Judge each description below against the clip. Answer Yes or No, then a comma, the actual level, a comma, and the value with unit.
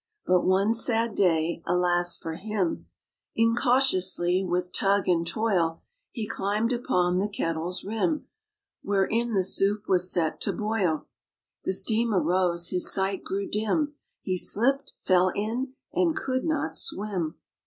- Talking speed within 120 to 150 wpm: Yes, slow, 135 wpm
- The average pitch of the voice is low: No, high, 195 Hz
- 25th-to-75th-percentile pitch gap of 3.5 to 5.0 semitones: Yes, average, 4.0 semitones